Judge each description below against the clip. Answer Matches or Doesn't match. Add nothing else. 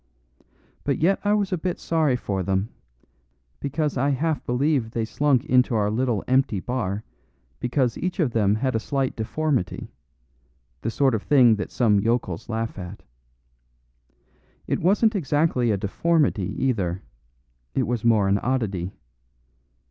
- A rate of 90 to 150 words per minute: Matches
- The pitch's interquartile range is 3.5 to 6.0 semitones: Matches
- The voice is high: Doesn't match